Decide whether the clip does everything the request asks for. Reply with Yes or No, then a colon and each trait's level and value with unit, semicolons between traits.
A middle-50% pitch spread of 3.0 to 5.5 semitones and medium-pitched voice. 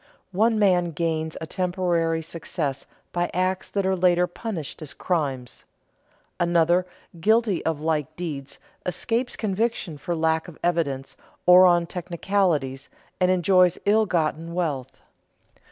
No: narrow, 2.5 semitones; medium, 175 Hz